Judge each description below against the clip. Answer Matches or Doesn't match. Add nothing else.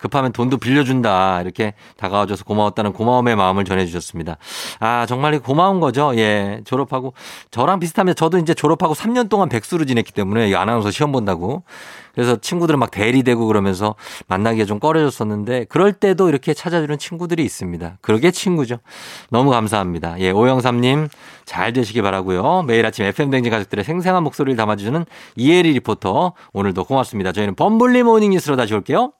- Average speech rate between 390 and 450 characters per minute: Matches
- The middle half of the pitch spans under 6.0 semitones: Doesn't match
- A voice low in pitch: Matches